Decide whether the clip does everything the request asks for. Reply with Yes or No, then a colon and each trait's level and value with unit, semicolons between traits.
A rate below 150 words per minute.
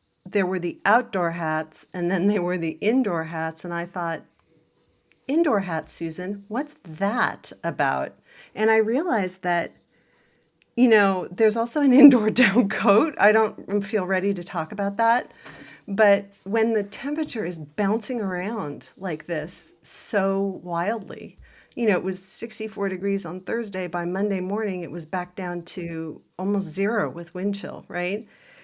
No: average, 155 wpm